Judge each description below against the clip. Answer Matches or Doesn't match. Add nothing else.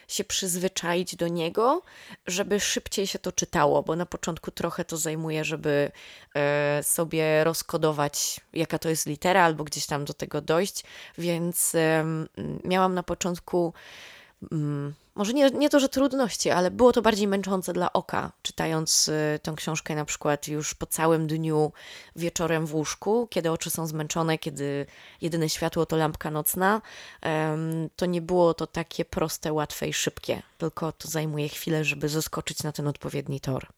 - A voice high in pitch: Doesn't match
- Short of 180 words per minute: Matches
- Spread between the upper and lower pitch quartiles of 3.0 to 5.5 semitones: Doesn't match